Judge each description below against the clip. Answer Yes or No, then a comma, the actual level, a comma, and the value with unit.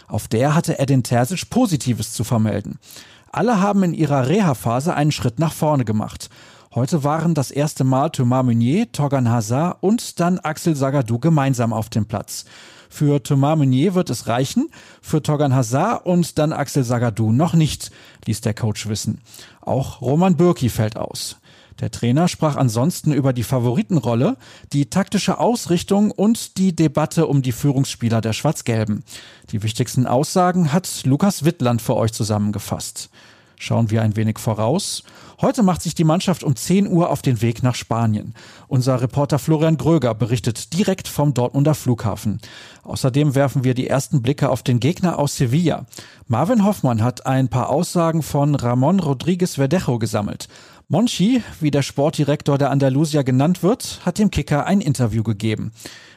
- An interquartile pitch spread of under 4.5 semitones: No, wide, 5.5 semitones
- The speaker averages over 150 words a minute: Yes, average, 160 wpm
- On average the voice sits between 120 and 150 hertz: Yes, medium, 140 Hz